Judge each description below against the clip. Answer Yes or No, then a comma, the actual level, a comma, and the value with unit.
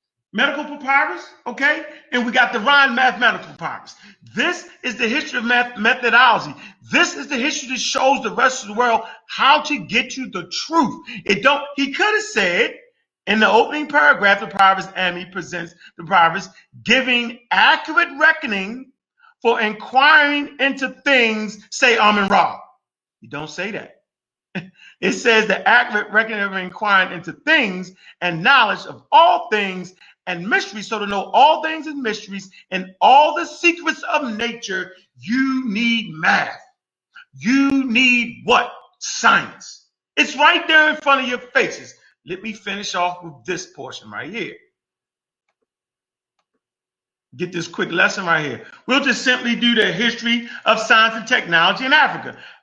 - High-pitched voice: Yes, high, 245 Hz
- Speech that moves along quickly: No, average, 155 wpm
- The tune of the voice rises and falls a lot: Yes, wide, 6.3 semitones